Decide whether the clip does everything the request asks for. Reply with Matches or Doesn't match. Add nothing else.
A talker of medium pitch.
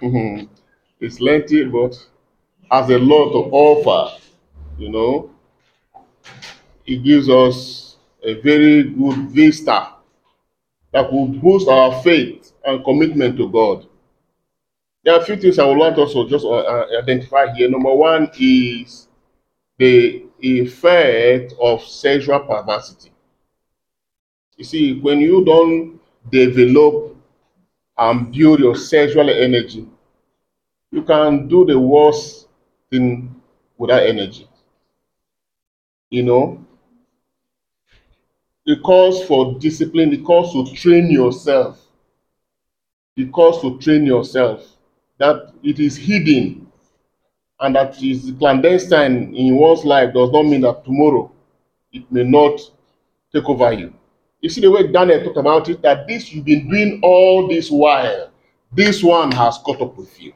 Matches